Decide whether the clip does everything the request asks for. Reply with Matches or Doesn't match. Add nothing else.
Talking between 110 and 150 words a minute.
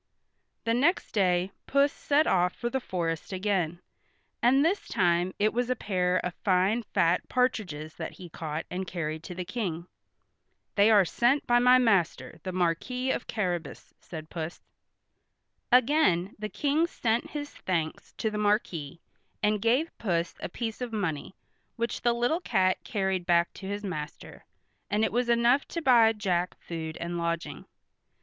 Doesn't match